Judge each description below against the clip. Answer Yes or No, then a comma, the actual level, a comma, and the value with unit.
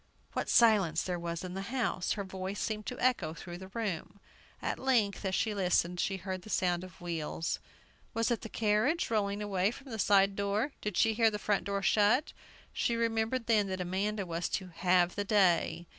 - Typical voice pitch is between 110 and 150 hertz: No, high, 200 Hz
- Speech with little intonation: No, average, 3.3 semitones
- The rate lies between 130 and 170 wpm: No, average, 200 wpm